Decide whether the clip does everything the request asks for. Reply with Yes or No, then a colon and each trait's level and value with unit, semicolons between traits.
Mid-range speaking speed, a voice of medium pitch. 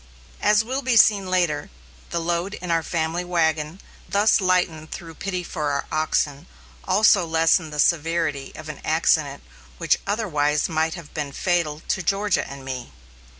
Yes: average, 155 wpm; medium, 170 Hz